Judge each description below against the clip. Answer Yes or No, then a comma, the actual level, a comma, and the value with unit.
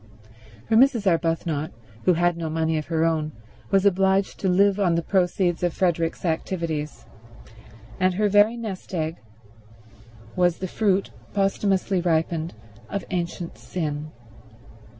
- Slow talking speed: Yes, slow, 130 wpm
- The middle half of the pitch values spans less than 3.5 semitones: Yes, average, 2.9 semitones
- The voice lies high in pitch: No, medium, 175 Hz